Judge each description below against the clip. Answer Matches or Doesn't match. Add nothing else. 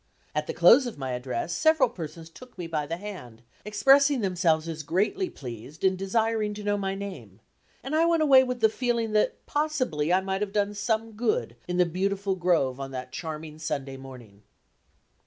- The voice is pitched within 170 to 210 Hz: Matches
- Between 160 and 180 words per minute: Doesn't match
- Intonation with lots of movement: Matches